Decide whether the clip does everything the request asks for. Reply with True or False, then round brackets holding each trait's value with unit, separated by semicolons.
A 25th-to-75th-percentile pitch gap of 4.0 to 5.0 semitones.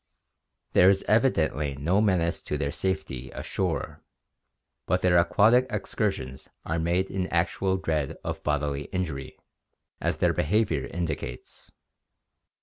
True (4.4 semitones)